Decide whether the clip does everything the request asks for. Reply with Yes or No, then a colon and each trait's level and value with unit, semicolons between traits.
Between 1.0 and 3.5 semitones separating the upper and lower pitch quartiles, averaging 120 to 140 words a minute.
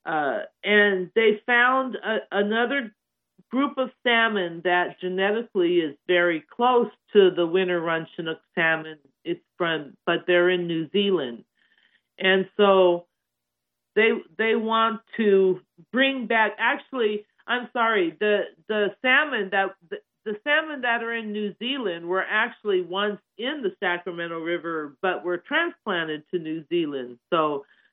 No: average, 4.8 semitones; slow, 135 wpm